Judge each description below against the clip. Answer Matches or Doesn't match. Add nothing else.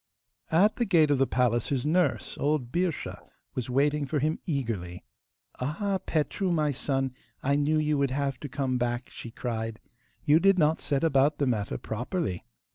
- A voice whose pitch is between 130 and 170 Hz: Matches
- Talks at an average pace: Matches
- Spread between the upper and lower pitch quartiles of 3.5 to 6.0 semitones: Matches